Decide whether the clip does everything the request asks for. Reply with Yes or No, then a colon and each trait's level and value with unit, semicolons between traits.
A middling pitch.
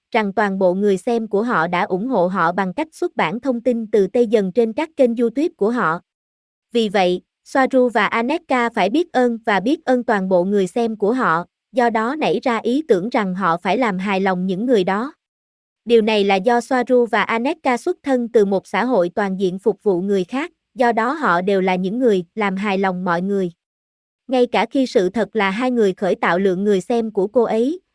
No: high, 220 Hz